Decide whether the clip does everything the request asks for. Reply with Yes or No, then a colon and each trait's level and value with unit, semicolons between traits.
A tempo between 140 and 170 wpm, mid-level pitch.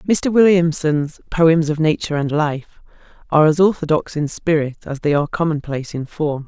Yes: average, 165 wpm; medium, 155 Hz